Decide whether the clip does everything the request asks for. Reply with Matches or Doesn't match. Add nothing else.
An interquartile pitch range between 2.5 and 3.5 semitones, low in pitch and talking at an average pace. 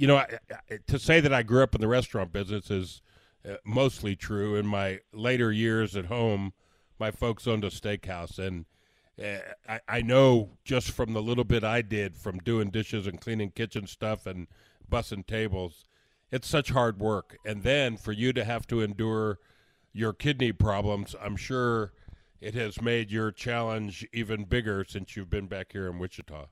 Matches